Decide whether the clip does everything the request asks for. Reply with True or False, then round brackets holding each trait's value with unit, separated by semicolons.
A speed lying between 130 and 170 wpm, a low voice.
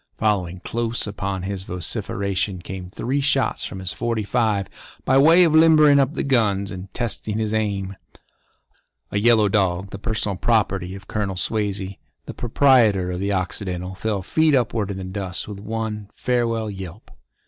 True (160 wpm; 105 Hz)